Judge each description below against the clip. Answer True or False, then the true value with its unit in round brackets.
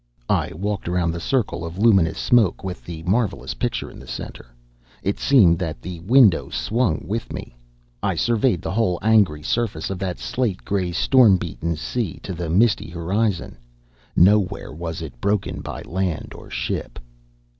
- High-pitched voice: False (95 Hz)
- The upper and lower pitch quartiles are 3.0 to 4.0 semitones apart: False (4.6 semitones)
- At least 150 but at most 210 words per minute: True (165 wpm)